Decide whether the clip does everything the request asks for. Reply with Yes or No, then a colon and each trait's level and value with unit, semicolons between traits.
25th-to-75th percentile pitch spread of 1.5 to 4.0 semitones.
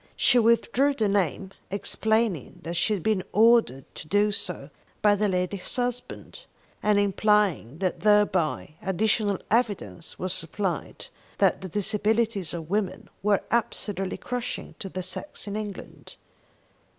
Yes: average, 2.9 semitones